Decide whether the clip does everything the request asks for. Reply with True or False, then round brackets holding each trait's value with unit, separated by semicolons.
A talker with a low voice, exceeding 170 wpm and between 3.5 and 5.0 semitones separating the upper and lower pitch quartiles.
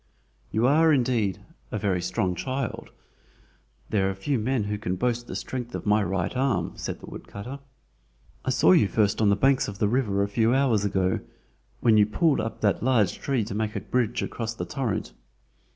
True (110 Hz; 200 wpm; 3.9 semitones)